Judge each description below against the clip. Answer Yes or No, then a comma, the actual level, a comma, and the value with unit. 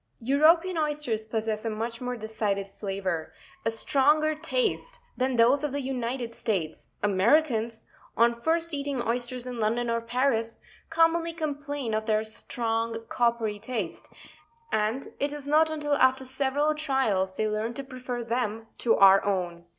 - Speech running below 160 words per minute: Yes, average, 150 wpm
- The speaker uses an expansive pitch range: No, average, 4.6 semitones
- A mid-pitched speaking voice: No, high, 240 Hz